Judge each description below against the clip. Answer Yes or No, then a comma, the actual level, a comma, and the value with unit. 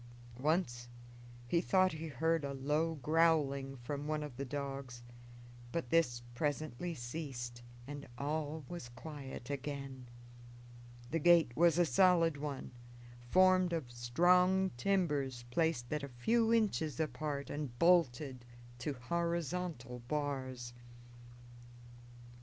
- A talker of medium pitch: Yes, medium, 145 Hz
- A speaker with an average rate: No, slow, 115 wpm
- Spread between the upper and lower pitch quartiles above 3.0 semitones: Yes, average, 4.3 semitones